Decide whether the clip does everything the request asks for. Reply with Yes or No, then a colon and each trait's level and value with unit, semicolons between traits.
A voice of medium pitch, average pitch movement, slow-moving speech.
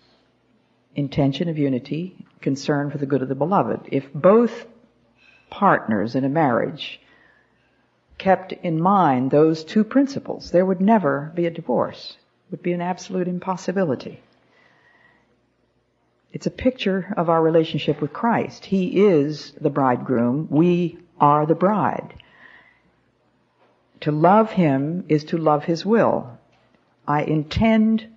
Yes: medium, 170 Hz; average, 4.6 semitones; slow, 130 wpm